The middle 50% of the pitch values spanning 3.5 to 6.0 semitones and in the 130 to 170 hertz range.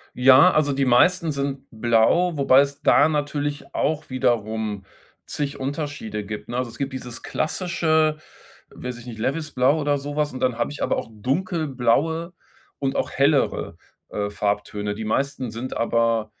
Yes: average, 4.1 semitones; low, 135 Hz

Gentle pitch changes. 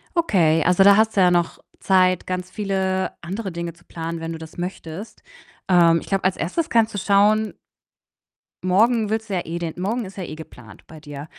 No: average, 3.4 semitones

